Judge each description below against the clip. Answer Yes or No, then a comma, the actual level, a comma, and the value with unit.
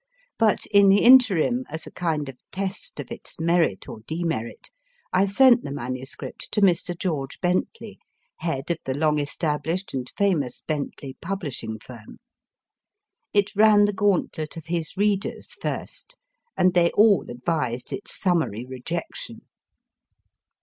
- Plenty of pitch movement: Yes, wide, 6.0 semitones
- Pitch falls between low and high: Yes, medium, 170 Hz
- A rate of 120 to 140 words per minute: Yes, slow, 135 wpm